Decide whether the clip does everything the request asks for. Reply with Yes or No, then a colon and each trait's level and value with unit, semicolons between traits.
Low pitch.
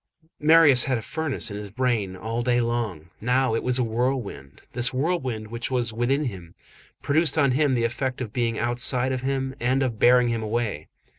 Yes: low, 120 Hz